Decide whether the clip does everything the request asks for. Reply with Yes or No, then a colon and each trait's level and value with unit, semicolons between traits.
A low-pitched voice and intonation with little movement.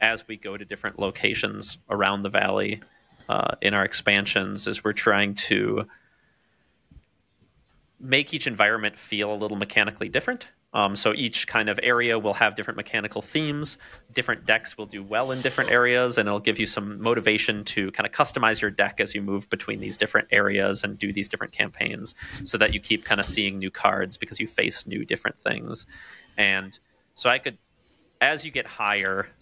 Yes: low, 105 Hz; narrow, 2.3 semitones